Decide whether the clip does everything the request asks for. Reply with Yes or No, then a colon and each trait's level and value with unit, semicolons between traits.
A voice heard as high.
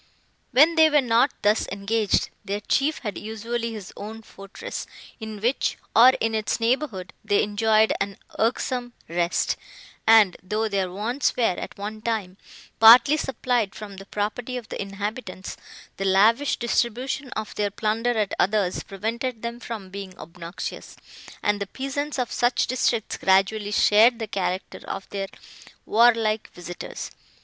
Yes: high, 220 Hz